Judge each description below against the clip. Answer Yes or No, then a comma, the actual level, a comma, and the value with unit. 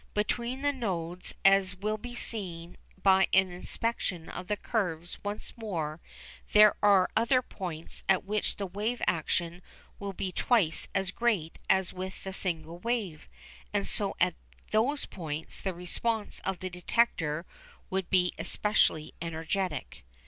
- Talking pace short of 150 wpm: Yes, average, 140 wpm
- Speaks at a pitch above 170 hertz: Yes, high, 190 Hz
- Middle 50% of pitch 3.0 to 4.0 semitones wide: Yes, average, 3.6 semitones